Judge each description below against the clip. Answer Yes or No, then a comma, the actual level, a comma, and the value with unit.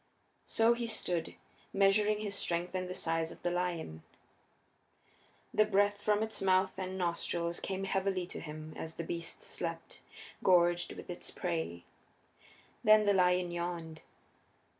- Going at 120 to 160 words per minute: Yes, average, 140 wpm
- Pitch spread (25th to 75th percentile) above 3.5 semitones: No, average, 2.9 semitones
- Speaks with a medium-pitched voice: Yes, medium, 180 Hz